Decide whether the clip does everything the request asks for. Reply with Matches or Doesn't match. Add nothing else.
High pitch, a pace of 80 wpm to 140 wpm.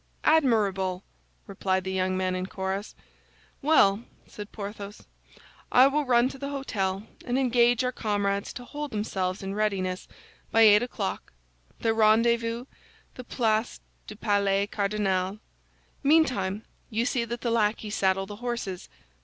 Matches